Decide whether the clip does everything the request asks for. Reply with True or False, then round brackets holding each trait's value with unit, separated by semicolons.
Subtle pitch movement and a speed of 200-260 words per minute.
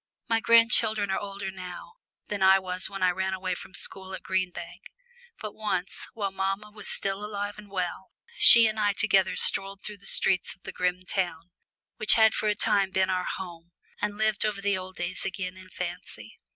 True (2.1 semitones; 205 wpm)